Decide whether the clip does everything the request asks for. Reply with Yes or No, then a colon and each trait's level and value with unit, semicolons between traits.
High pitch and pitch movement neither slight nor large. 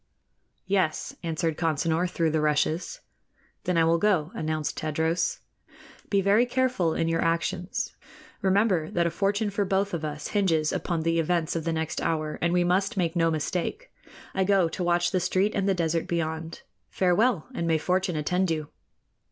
No: medium, 170 Hz; average, 3.0 semitones